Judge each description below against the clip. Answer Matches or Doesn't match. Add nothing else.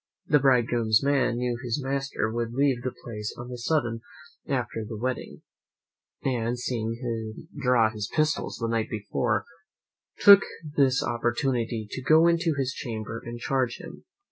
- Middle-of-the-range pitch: Doesn't match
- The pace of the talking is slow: Doesn't match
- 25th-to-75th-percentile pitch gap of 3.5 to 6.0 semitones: Doesn't match